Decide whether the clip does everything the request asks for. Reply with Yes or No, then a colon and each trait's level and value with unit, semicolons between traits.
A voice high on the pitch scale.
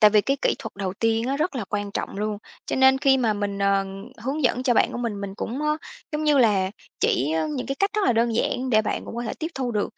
Yes: high, 230 Hz